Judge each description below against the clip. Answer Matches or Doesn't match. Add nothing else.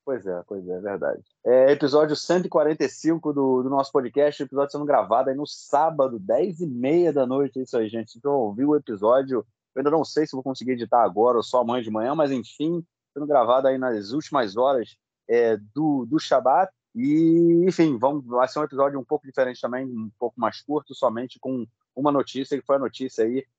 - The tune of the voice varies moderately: Matches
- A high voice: Doesn't match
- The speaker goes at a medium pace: Doesn't match